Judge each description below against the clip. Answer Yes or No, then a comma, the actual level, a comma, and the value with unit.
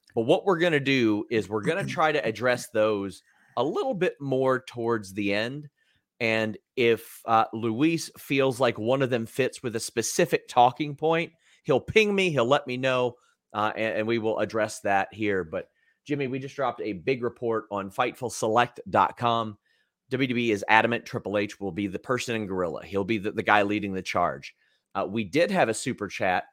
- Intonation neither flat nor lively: Yes, average, 3.8 semitones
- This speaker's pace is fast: No, average, 195 wpm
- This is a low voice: Yes, low, 115 Hz